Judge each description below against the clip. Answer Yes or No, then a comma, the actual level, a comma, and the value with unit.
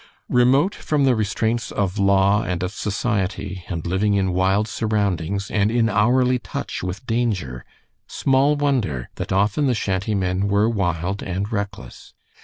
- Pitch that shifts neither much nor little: Yes, average, 3.7 semitones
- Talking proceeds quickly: No, average, 150 wpm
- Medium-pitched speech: No, low, 100 Hz